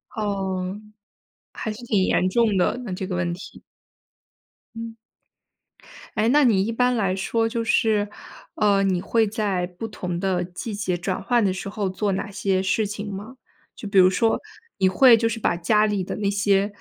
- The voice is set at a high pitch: Yes, high, 200 Hz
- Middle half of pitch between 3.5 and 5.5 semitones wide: No, average, 3.0 semitones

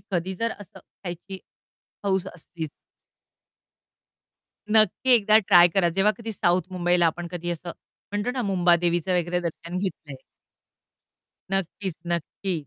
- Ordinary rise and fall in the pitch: No, narrow, 2.3 semitones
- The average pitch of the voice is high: No, medium, 180 Hz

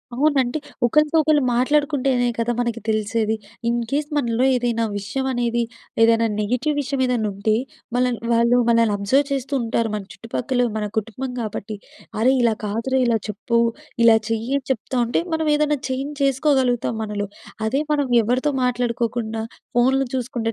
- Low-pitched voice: No, high, 240 Hz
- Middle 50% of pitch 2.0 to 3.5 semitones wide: Yes, average, 2.8 semitones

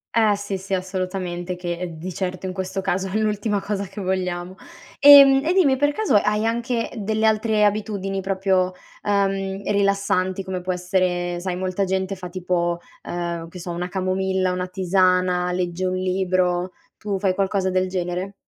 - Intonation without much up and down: Yes, narrow, 1.7 semitones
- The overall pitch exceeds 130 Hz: Yes, high, 190 Hz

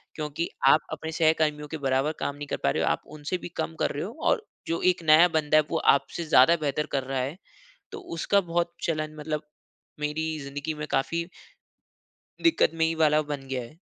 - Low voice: No, medium, 155 Hz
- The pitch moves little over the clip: Yes, narrow, 2.1 semitones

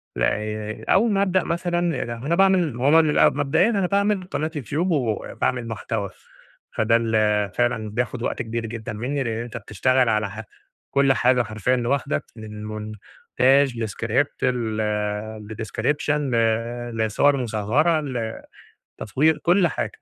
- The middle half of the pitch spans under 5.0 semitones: No, wide, 5.5 semitones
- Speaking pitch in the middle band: No, low, 125 Hz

